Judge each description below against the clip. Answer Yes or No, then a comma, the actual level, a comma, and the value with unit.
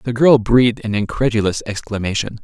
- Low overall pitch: Yes, low, 110 Hz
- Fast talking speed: No, average, 150 wpm